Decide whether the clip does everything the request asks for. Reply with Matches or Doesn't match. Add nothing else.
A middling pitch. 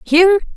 Doesn't match